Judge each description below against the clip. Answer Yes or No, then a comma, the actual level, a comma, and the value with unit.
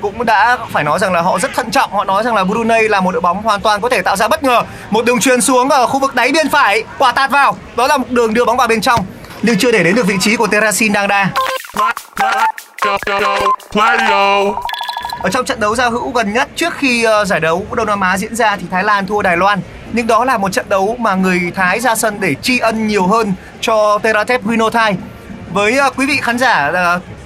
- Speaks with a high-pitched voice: Yes, high, 225 Hz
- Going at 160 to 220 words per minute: No, average, 240 wpm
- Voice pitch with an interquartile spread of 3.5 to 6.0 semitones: Yes, average, 4.3 semitones